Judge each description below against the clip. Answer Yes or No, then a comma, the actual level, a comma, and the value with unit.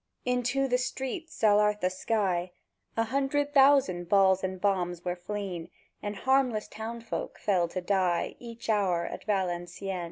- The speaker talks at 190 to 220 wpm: No, average, 140 wpm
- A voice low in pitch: No, high, 205 Hz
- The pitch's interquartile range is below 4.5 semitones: No, average, 5.1 semitones